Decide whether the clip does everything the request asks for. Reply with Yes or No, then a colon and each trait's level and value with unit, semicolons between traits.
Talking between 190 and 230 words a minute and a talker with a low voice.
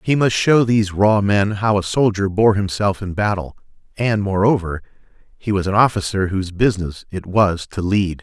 No: average, 180 wpm; low, 100 Hz